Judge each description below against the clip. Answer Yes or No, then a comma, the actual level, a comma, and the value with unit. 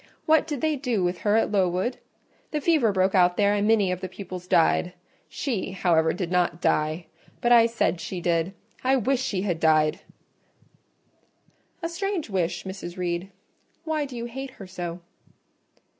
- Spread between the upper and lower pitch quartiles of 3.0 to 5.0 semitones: No, wide, 5.4 semitones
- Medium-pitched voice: No, high, 195 Hz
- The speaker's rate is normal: Yes, average, 165 wpm